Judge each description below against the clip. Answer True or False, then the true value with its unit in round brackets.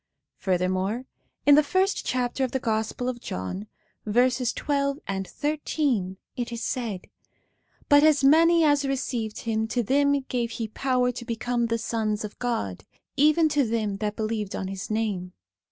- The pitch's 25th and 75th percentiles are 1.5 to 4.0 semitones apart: False (4.5 semitones)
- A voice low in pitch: False (240 Hz)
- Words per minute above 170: False (160 wpm)